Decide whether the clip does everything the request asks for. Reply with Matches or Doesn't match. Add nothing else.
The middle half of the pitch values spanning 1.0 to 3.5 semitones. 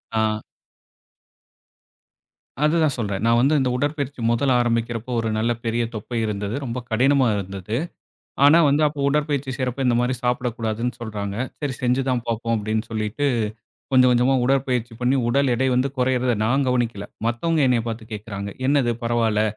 Matches